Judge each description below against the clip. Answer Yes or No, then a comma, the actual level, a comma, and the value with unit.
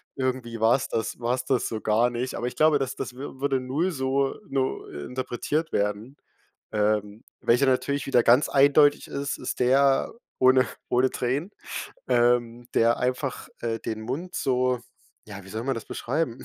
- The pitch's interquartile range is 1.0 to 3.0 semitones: Yes, average, 2.7 semitones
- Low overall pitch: Yes, low, 125 Hz